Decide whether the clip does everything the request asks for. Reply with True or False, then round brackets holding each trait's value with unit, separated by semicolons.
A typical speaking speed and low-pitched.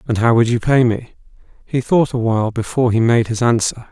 False (230 wpm; 120 Hz)